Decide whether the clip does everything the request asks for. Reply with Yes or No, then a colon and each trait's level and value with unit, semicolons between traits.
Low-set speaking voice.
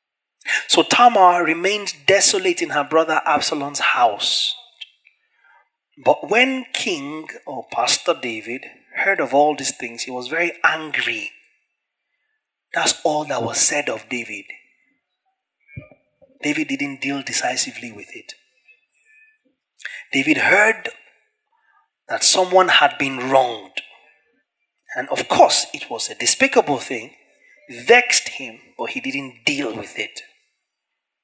No: high, 200 Hz